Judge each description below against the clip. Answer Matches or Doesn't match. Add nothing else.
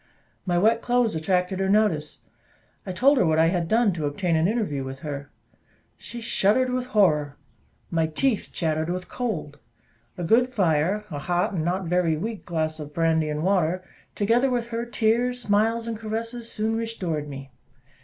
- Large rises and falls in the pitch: Matches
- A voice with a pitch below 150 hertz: Doesn't match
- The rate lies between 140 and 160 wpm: Doesn't match